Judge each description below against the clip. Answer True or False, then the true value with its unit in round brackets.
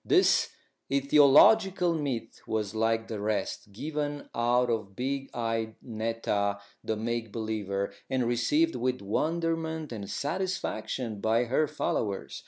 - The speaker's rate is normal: False (120 wpm)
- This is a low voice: True (120 Hz)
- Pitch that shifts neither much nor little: True (4.9 semitones)